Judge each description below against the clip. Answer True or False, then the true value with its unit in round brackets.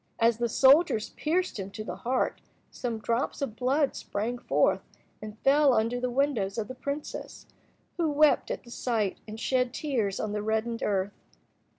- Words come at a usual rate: True (175 wpm)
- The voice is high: True (235 Hz)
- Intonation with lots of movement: False (4.2 semitones)